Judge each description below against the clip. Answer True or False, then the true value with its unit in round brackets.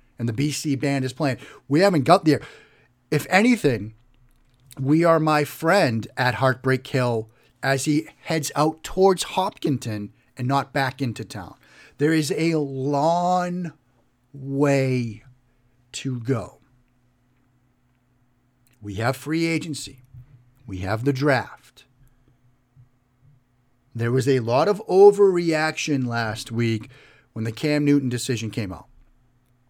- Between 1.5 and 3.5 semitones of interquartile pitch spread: True (3.1 semitones)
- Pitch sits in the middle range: False (130 Hz)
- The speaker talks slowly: True (120 wpm)